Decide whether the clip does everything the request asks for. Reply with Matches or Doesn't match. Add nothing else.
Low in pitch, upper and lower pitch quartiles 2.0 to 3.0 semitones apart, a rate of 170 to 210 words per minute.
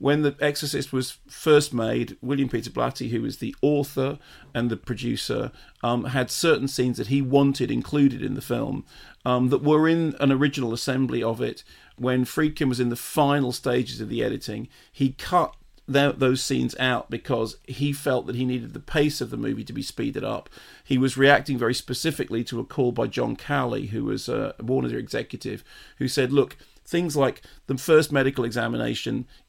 Matches